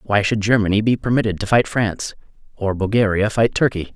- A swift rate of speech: No, average, 180 wpm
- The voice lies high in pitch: No, low, 105 Hz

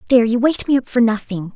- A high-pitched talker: Yes, high, 240 Hz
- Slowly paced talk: No, fast, 270 wpm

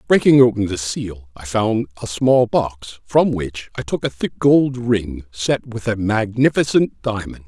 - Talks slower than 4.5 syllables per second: Yes, 4.1 syllables/s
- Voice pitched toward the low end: Yes, low, 110 Hz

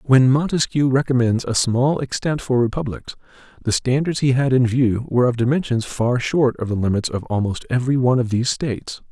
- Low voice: Yes, low, 125 Hz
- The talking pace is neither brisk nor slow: Yes, average, 190 wpm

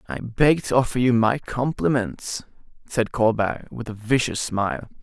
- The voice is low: Yes, low, 120 Hz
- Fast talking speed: No, average, 155 wpm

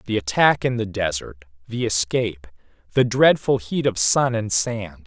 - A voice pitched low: Yes, low, 105 Hz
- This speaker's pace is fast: No, average, 165 wpm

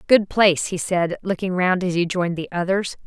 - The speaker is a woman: Yes, female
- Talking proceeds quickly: Yes, fast, 215 wpm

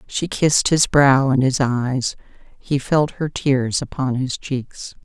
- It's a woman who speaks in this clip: Yes, female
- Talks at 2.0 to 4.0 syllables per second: Yes, 3.6 syllables/s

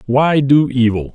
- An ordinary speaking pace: Yes, average, 155 wpm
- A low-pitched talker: Yes, low, 130 Hz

